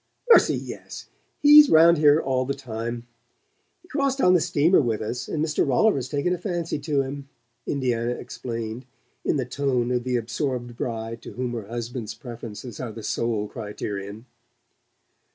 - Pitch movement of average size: Yes, average, 4.1 semitones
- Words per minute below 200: Yes, average, 160 wpm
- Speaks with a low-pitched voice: Yes, low, 125 Hz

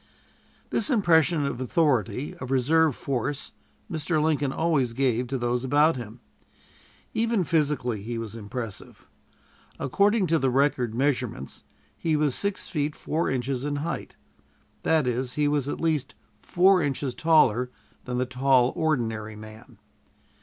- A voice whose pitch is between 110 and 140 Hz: Yes, low, 135 Hz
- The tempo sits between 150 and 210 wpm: No, average, 140 wpm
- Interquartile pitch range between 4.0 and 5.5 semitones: Yes, average, 4.3 semitones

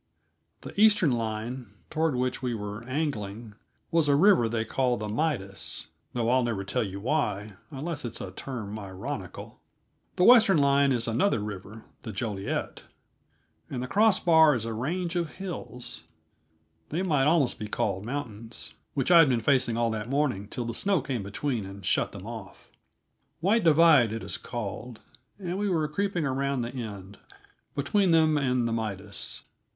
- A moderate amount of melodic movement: No, wide, 6.2 semitones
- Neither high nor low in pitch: No, low, 125 Hz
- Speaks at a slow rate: No, average, 165 wpm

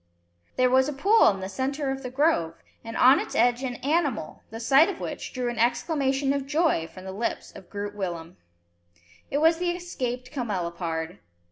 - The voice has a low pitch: No, very high, 255 Hz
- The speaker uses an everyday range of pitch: No, wide, 5.8 semitones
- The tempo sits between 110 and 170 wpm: No, average, 190 wpm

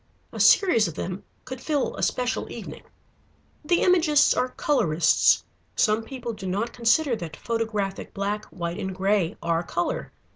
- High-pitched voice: Yes, high, 215 Hz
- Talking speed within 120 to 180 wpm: Yes, average, 150 wpm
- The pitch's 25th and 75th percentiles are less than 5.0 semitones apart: No, wide, 5.4 semitones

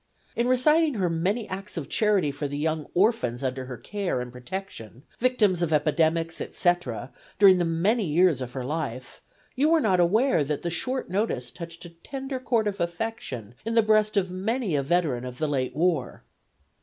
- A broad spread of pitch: Yes, wide, 6.8 semitones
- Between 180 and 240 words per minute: Yes, average, 185 wpm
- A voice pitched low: No, medium, 175 Hz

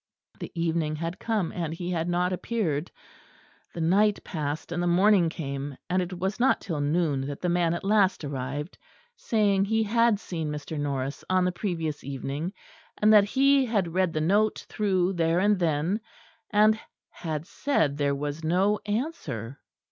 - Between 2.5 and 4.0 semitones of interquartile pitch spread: No, average, 5.0 semitones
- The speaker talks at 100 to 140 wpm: No, average, 170 wpm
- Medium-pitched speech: Yes, medium, 175 Hz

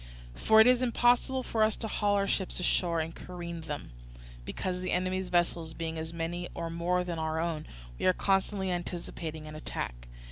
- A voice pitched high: No, medium, 175 Hz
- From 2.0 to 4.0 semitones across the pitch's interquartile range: Yes, average, 2.9 semitones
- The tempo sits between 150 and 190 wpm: Yes, average, 185 wpm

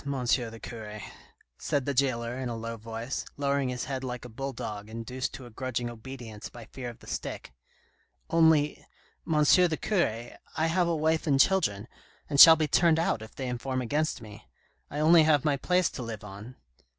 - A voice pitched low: Yes, low, 130 Hz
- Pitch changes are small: No, average, 4.6 semitones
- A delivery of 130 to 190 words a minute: No, average, 200 wpm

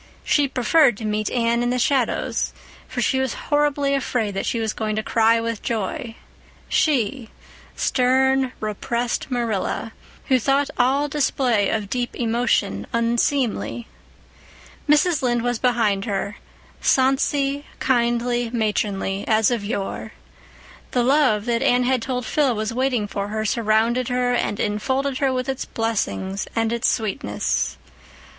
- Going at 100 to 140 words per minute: Yes, slow, 135 wpm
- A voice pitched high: Yes, high, 240 Hz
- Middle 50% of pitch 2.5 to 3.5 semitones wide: Yes, average, 3.2 semitones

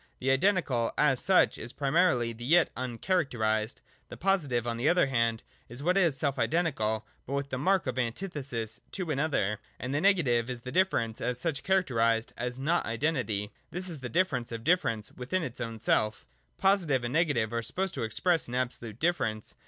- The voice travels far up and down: Yes, wide, 6.4 semitones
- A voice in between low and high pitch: No, low, 130 Hz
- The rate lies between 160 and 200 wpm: Yes, average, 185 wpm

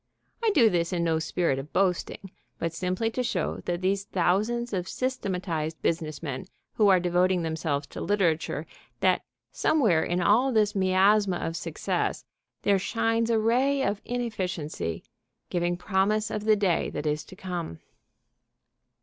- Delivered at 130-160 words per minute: Yes, average, 150 wpm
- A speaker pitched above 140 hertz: Yes, medium, 185 Hz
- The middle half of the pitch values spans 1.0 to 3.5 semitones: No, average, 4.3 semitones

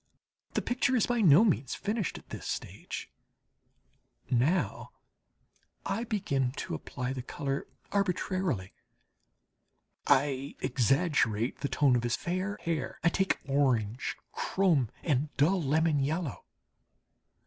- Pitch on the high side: No, medium, 145 Hz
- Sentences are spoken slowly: Yes, slow, 115 wpm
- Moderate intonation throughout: No, wide, 6.0 semitones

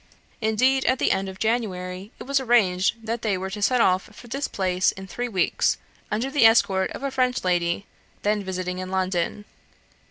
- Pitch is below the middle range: No, high, 205 Hz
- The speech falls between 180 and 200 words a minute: Yes, average, 190 wpm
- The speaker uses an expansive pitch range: No, average, 4.4 semitones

